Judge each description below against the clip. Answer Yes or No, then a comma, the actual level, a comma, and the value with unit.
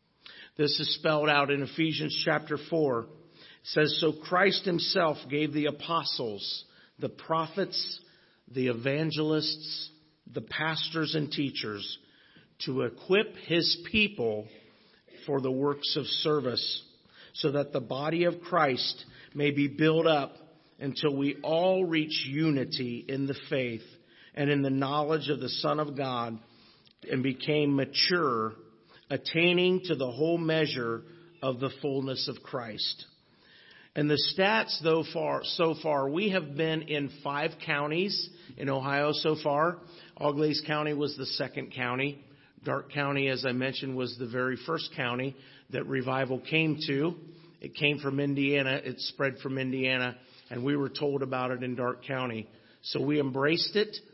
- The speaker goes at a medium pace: Yes, average, 145 wpm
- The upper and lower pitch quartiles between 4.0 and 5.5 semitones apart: No, average, 3.2 semitones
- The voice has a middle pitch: Yes, medium, 145 Hz